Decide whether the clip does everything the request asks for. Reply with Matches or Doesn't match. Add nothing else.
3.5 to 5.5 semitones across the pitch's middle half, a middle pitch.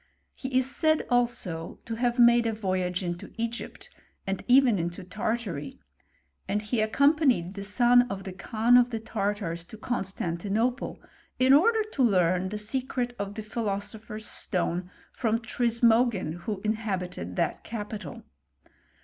Doesn't match